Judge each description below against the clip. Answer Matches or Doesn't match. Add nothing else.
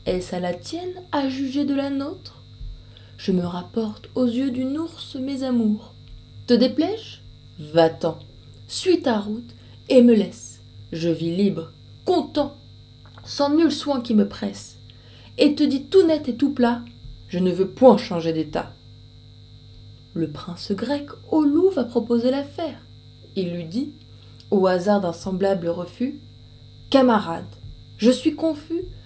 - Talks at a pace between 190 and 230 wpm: Doesn't match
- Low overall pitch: Doesn't match